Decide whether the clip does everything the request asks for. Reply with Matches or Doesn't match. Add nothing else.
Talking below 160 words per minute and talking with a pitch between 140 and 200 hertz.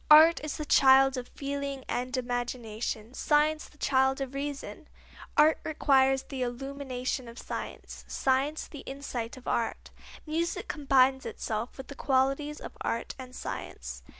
Doesn't match